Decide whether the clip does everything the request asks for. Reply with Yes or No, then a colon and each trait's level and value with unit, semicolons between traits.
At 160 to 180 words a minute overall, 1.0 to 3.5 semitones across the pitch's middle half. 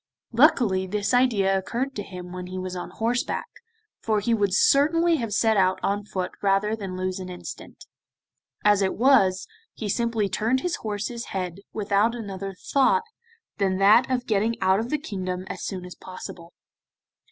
No: average, 170 wpm; average, 3.9 semitones